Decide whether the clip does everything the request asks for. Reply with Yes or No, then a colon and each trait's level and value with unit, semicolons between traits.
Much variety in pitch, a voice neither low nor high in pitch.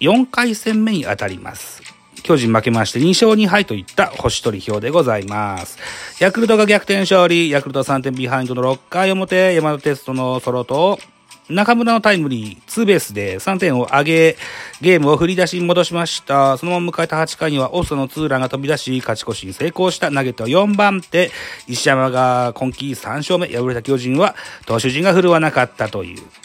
Yes: wide, 6.3 semitones; medium, 150 Hz